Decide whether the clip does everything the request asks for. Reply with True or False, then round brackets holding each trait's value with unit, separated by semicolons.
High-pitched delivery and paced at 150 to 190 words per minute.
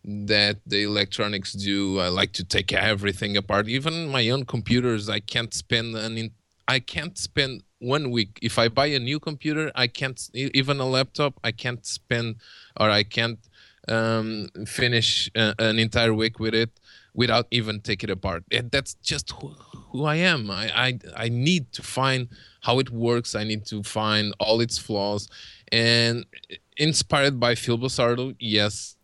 False (115 Hz; 170 wpm)